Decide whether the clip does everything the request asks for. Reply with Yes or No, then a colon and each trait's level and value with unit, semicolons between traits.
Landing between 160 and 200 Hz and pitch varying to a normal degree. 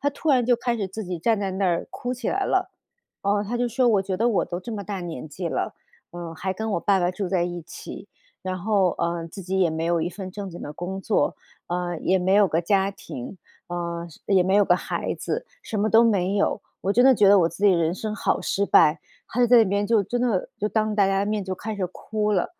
Yes: high, 195 Hz; average, 3.5 semitones